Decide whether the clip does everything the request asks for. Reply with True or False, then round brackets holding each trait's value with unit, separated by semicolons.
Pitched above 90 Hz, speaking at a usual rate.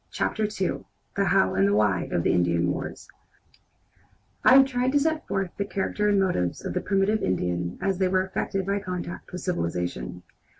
True (185 Hz; 180 wpm)